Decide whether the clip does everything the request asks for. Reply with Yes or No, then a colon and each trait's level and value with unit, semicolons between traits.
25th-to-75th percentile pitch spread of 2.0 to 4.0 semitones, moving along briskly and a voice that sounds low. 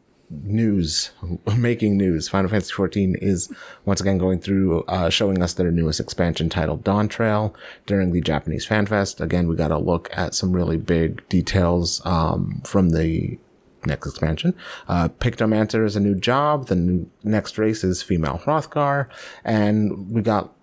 No: average, 3.7 semitones; average, 165 wpm; very low, 95 Hz